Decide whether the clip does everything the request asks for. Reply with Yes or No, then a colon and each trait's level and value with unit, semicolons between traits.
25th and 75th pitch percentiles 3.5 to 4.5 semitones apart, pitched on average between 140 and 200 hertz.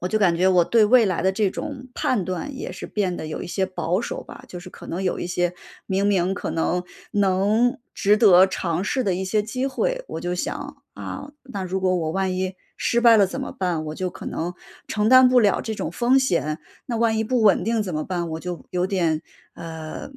Yes: average, 3.8 semitones; high, 190 Hz